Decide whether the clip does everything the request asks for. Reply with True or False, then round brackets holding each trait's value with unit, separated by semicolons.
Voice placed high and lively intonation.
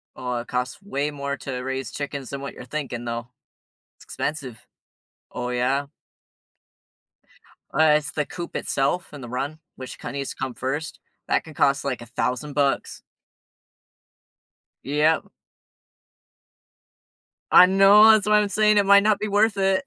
False (140 Hz; 5.9 semitones)